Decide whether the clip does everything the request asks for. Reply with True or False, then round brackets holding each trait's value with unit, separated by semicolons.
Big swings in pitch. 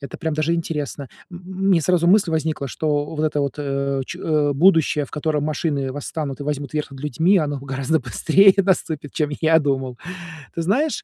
False (2.9 semitones)